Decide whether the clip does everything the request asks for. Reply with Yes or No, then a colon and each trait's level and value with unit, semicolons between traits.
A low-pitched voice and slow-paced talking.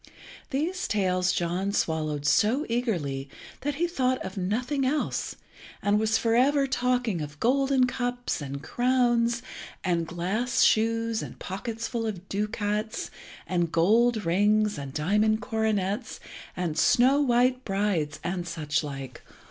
No: high, 215 Hz; slow, 130 wpm